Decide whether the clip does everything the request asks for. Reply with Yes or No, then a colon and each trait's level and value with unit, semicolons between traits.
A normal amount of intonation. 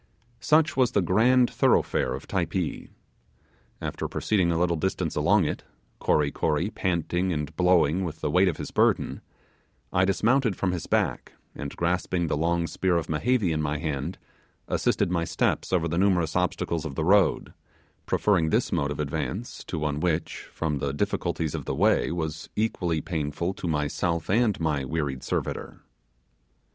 Yes: average, 3.5 semitones